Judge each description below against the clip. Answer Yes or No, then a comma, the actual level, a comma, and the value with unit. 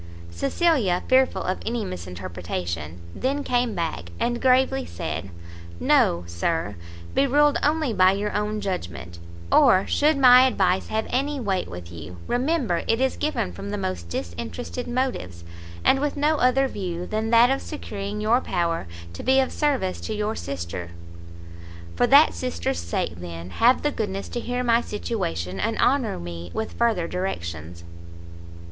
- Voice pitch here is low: No, high, 195 Hz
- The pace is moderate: Yes, average, 155 wpm